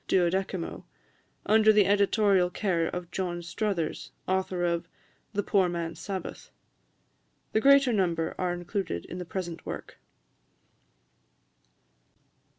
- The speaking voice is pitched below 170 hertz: No, medium, 185 Hz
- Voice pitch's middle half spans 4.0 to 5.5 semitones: No, average, 2.7 semitones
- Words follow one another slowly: Yes, slow, 110 wpm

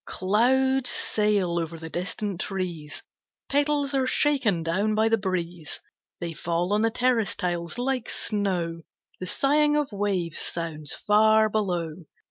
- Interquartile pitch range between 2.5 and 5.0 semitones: No, wide, 5.6 semitones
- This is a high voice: Yes, high, 200 Hz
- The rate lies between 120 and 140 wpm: Yes, slow, 135 wpm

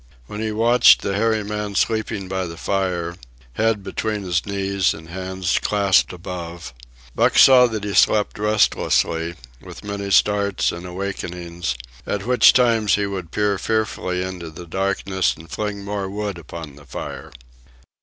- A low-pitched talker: Yes, low, 100 Hz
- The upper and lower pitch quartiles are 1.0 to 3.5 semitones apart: Yes, average, 2.9 semitones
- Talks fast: No, average, 155 wpm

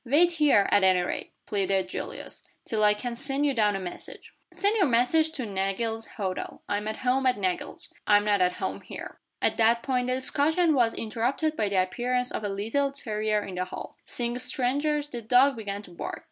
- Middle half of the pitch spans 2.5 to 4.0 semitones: No, average, 4.8 semitones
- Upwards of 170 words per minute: Yes, average, 200 wpm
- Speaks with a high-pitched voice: Yes, high, 230 Hz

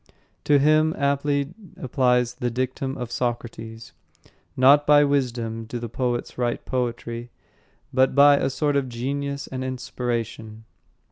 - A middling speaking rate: No, slow, 130 wpm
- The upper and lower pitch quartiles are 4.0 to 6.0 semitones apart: No, average, 2.9 semitones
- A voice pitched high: No, low, 130 Hz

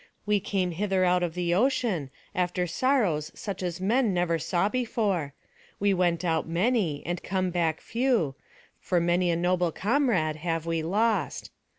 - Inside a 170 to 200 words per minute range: No, average, 160 wpm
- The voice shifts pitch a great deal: No, average, 3.6 semitones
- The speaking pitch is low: No, medium, 180 Hz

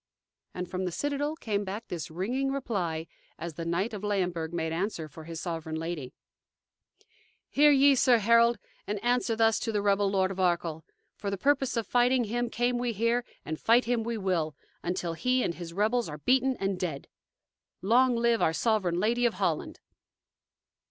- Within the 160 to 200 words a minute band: Yes, average, 180 wpm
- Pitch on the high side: Yes, high, 205 Hz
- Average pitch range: No, wide, 5.8 semitones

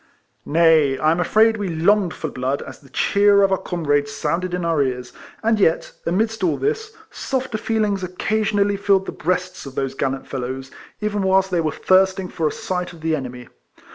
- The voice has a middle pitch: Yes, medium, 180 Hz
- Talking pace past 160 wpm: Yes, average, 195 wpm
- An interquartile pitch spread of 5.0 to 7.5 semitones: Yes, average, 5.3 semitones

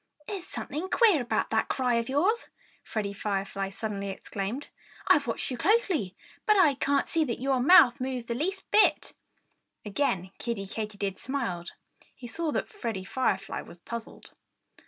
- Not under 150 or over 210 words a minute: Yes, average, 155 wpm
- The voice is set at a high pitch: Yes, high, 245 Hz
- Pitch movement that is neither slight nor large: No, wide, 6.9 semitones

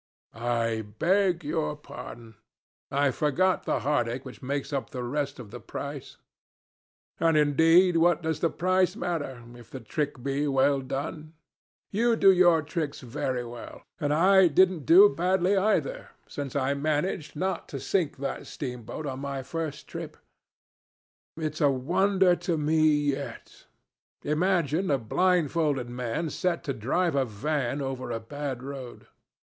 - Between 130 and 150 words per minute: Yes, average, 145 wpm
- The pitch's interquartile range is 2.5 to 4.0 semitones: No, average, 4.6 semitones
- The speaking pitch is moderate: Yes, medium, 145 Hz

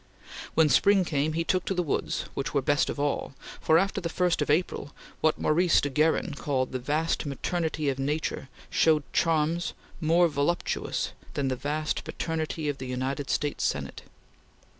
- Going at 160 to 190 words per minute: Yes, average, 170 wpm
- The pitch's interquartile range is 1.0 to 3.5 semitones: Yes, narrow, 2.6 semitones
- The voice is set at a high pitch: No, medium, 155 Hz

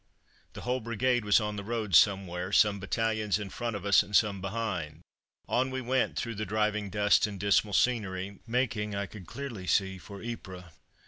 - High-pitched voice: No, low, 105 Hz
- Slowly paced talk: No, average, 185 wpm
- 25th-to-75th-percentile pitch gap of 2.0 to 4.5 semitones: Yes, average, 2.7 semitones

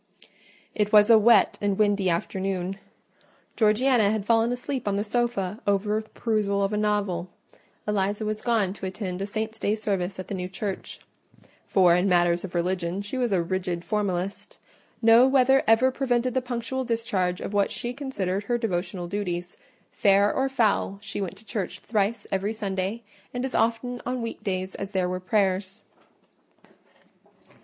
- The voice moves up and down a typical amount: Yes, average, 3.3 semitones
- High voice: Yes, high, 205 Hz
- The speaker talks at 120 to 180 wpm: Yes, average, 165 wpm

